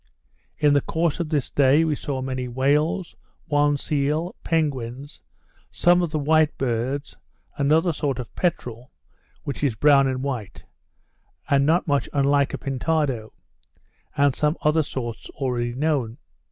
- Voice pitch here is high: No, medium, 140 Hz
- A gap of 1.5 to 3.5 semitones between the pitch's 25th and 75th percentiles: Yes, average, 2.9 semitones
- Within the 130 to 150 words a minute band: Yes, average, 140 wpm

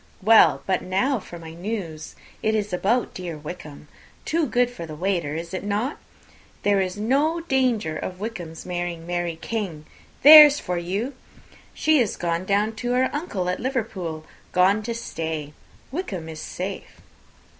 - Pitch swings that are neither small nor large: No, wide, 5.8 semitones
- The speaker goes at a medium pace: Yes, average, 155 wpm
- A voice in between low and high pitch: No, high, 195 Hz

